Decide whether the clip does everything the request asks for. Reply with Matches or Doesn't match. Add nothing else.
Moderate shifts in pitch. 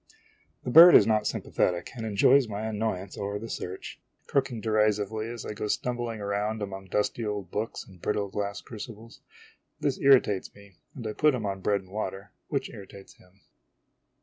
Doesn't match